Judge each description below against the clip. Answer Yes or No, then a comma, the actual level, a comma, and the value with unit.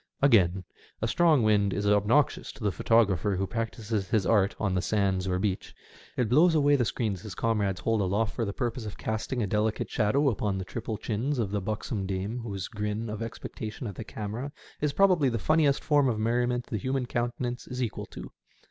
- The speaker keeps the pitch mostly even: No, average, 3.4 semitones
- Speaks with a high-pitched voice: No, low, 110 Hz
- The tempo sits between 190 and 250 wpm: Yes, average, 200 wpm